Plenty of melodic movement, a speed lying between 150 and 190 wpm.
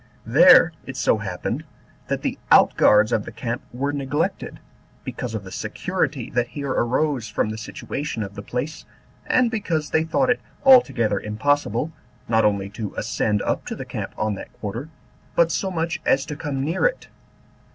Yes: wide, 6.6 semitones; average, 175 wpm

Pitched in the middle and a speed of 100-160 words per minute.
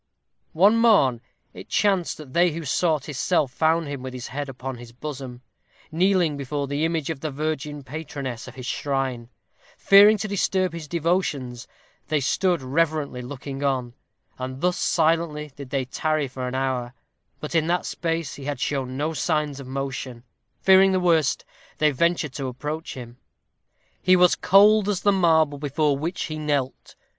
No: medium, 150 Hz; average, 170 wpm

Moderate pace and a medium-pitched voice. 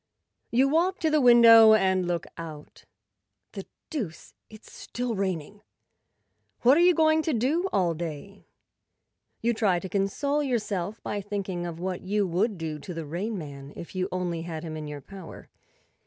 No: average, 170 wpm; high, 195 Hz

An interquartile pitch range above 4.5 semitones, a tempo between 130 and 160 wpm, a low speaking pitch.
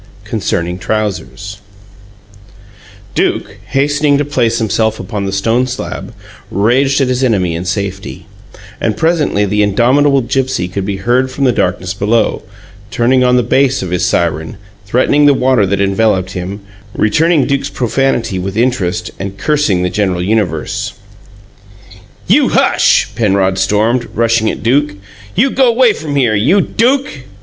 Yes: wide, 5.5 semitones; average, 145 wpm; low, 115 Hz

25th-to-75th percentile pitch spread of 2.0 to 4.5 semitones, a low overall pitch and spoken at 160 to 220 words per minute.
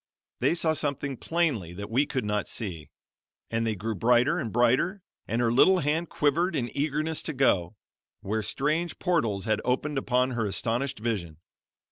No: wide, 5.5 semitones; low, 125 Hz; average, 165 wpm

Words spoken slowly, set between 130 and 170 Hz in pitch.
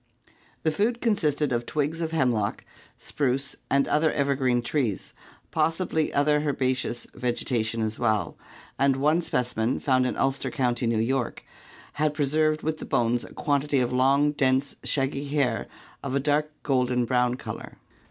No: average, 150 wpm; low, 135 Hz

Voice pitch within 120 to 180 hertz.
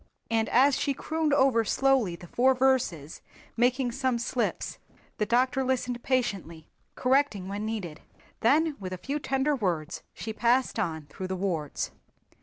No: high, 240 Hz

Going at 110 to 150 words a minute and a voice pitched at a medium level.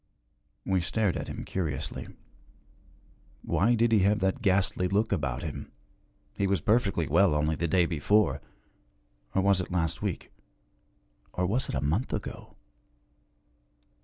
No: average, 140 wpm; very low, 95 Hz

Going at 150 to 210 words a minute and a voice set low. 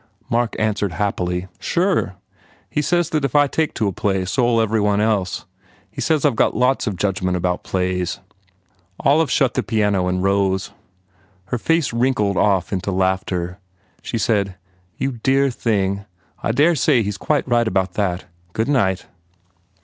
Yes: average, 170 wpm; low, 105 Hz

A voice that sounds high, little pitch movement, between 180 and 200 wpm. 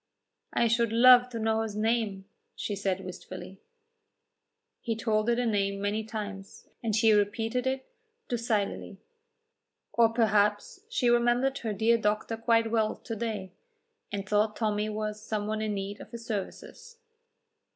No: high, 220 Hz; narrow, 2.1 semitones; average, 150 wpm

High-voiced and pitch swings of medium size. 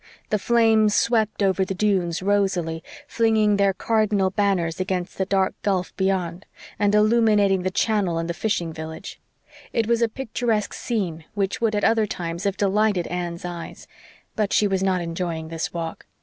Yes: high, 195 Hz; average, 3.3 semitones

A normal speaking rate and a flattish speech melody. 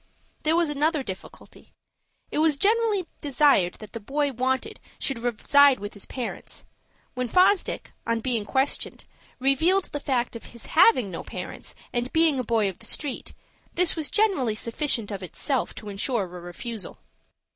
No: average, 160 wpm; average, 5.1 semitones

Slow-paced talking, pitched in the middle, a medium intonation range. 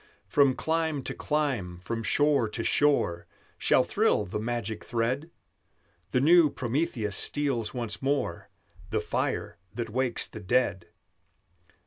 No: slow, 125 wpm; low, 125 Hz; average, 4.8 semitones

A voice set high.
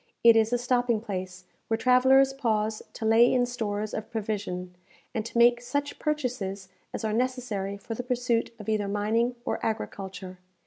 Yes: high, 225 Hz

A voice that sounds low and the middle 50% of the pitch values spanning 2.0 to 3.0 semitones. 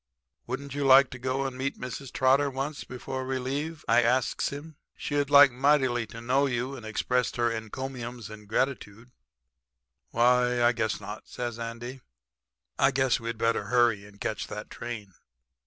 Yes: low, 125 Hz; narrow, 2.6 semitones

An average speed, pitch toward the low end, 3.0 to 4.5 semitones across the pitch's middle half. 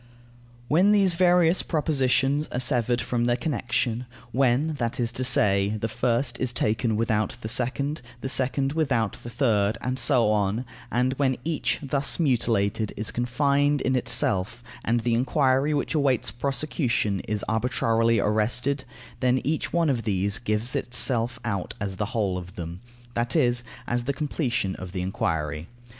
Yes: average, 155 wpm; low, 120 Hz; average, 4.0 semitones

